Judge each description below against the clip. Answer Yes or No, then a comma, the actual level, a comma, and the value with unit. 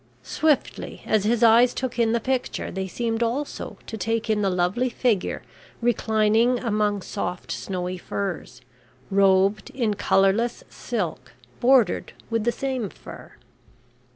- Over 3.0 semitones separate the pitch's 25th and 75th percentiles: Yes, average, 3.4 semitones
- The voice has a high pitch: Yes, high, 220 Hz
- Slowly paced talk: Yes, slow, 130 wpm